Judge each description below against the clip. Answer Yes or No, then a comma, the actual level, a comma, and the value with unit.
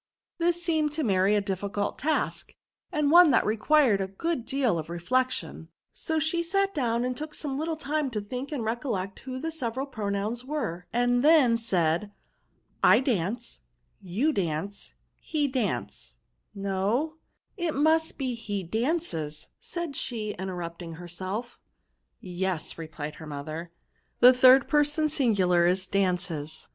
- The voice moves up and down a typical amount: No, wide, 7.9 semitones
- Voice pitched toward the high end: Yes, high, 230 Hz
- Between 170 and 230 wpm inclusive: No, average, 150 wpm